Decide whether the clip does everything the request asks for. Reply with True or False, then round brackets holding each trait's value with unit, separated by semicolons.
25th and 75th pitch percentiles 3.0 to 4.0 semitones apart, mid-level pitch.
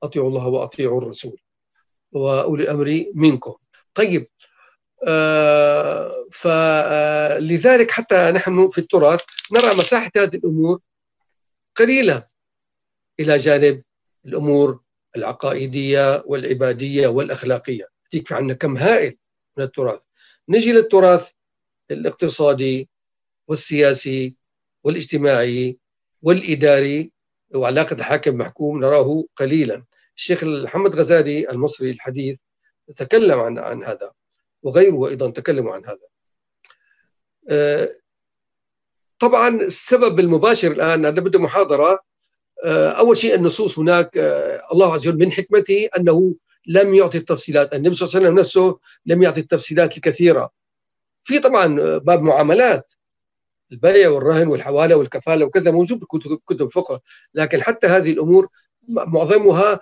False (5.2 semitones; 165 Hz)